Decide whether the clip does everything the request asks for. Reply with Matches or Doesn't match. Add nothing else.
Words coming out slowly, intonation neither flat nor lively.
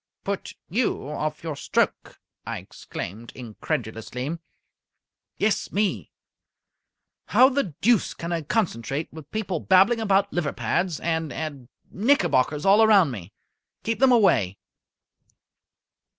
Doesn't match